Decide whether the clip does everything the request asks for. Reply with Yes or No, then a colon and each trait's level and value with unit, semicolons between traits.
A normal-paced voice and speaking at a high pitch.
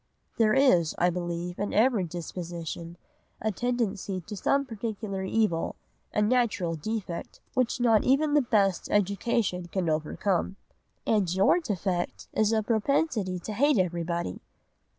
No: slow, 130 wpm; high, 200 Hz